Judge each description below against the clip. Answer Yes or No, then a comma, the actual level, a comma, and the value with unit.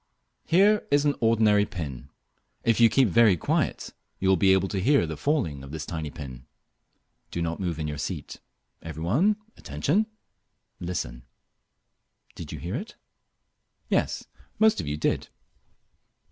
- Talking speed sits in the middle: Yes, average, 150 wpm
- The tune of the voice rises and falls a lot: Yes, wide, 8.6 semitones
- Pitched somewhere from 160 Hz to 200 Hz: No, very low, 95 Hz